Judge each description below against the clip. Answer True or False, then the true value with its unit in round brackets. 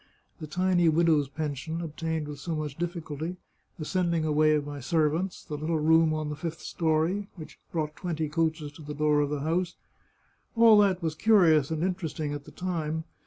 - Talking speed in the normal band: True (190 wpm)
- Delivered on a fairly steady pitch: True (2.1 semitones)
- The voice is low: False (160 Hz)